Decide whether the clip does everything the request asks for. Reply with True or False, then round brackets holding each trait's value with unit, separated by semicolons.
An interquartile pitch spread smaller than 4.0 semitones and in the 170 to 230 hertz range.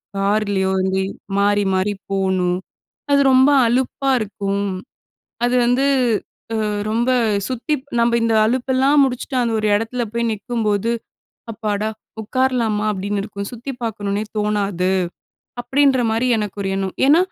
True (3.6 semitones; 220 Hz)